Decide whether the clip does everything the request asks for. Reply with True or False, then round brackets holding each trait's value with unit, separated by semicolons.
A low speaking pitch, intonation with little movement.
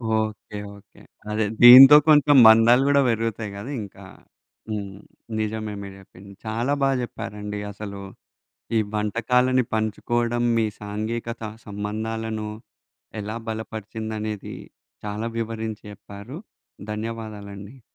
True (110 Hz; 2.0 semitones)